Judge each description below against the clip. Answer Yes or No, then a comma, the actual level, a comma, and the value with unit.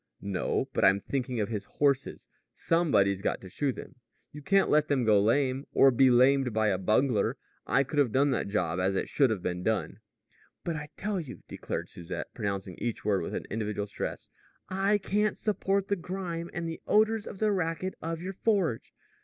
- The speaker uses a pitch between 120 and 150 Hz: Yes, low, 135 Hz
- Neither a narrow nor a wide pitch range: No, wide, 8.5 semitones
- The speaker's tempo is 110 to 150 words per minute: No, average, 195 wpm